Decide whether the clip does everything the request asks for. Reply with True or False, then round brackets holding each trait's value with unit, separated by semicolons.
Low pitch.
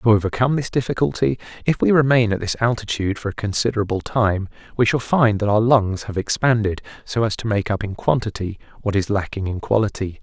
True (110 Hz)